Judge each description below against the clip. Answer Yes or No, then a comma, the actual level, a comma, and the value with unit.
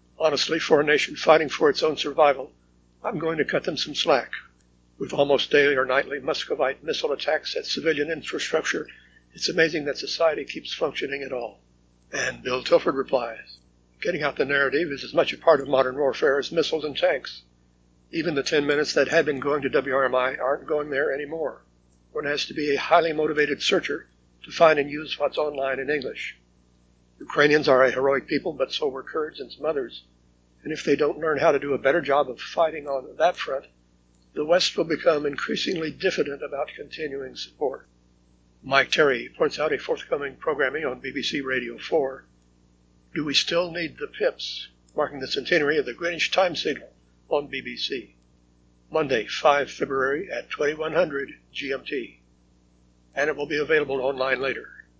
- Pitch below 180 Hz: Yes, low, 135 Hz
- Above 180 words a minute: No, average, 175 wpm